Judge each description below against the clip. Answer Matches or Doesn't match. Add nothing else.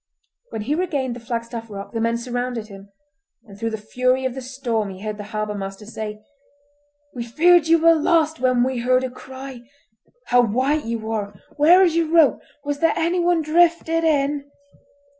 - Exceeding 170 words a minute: Matches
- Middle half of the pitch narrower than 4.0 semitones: Doesn't match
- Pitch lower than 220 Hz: Doesn't match